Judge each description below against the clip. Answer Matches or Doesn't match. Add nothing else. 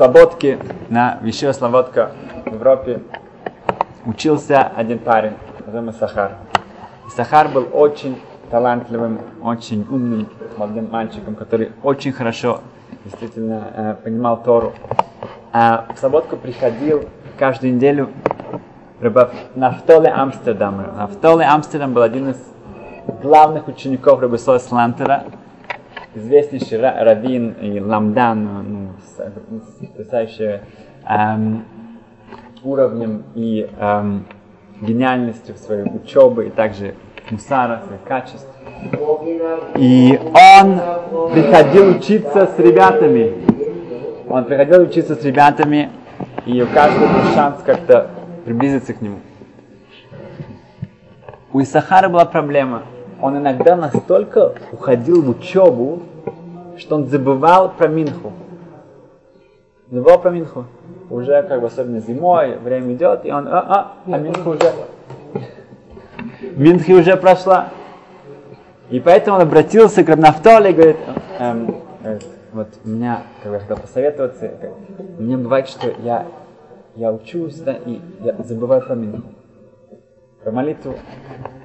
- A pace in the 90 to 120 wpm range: Matches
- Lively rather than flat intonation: Matches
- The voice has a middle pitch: Doesn't match